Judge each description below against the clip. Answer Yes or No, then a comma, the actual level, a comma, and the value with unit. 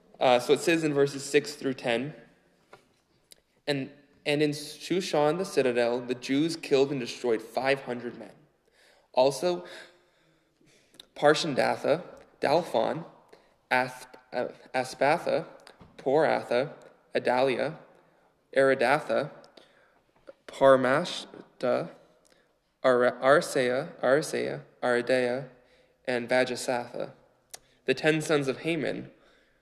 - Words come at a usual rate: No, slow, 85 wpm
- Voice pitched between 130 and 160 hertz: Yes, low, 135 Hz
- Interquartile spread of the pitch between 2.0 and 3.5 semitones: Yes, average, 2.9 semitones